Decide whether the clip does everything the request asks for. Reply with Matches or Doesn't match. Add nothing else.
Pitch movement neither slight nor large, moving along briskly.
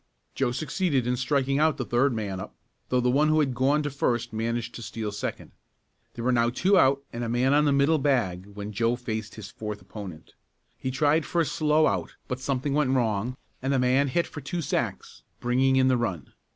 Matches